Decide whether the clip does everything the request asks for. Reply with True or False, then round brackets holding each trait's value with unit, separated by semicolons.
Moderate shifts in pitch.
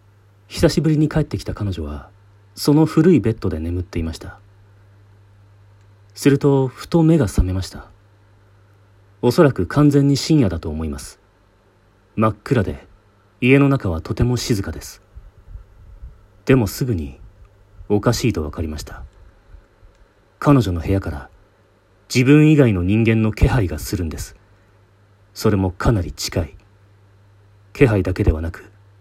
True (3.0 semitones)